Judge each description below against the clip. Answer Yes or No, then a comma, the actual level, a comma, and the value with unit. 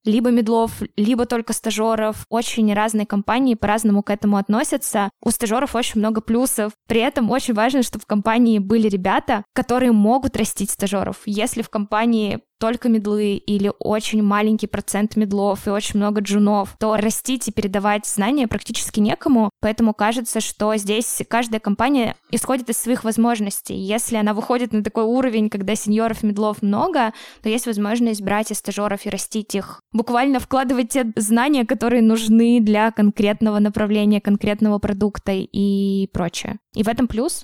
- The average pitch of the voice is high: Yes, high, 220 Hz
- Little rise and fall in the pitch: Yes, narrow, 2.1 semitones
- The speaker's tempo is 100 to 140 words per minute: No, average, 155 wpm